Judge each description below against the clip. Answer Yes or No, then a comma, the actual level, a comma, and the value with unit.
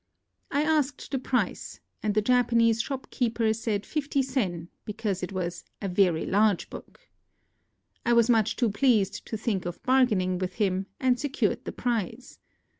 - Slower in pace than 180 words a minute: Yes, average, 155 wpm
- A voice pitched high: Yes, high, 225 Hz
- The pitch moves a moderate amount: Yes, average, 4.4 semitones